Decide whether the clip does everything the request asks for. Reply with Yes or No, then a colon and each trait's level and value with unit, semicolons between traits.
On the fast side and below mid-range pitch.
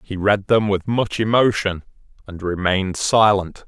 No: average, 145 wpm; low, 100 Hz